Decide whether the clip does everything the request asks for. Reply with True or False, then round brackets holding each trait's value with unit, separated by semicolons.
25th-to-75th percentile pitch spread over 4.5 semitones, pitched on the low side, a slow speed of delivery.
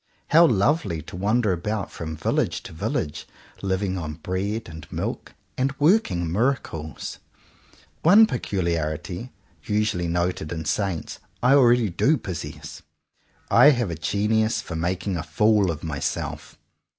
True (5.4 semitones; 95 Hz; 130 wpm)